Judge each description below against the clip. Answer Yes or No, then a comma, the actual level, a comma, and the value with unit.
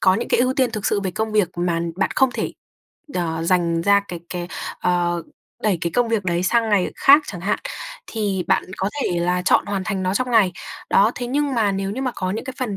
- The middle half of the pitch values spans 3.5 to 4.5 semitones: Yes, average, 4.1 semitones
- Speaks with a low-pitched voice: No, high, 195 Hz